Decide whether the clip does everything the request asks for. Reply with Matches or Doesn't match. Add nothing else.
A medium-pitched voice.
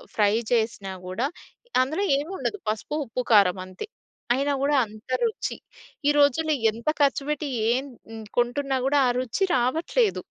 Doesn't match